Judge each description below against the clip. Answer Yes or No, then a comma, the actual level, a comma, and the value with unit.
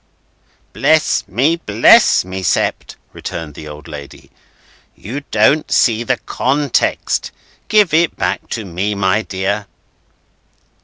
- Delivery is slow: Yes, slow, 115 wpm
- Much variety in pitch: Yes, wide, 6.4 semitones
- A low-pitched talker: Yes, low, 105 Hz